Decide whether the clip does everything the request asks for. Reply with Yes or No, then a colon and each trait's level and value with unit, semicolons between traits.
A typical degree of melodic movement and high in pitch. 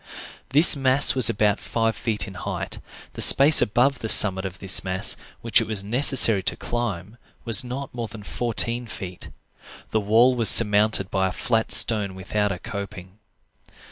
No: average, 3.5 semitones; low, 110 Hz